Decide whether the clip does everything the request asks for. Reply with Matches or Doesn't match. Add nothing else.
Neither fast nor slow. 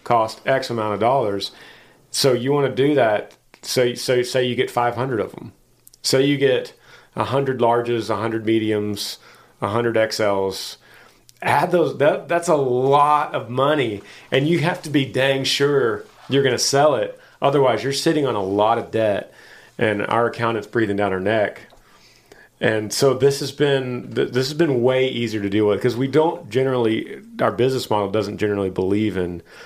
Matches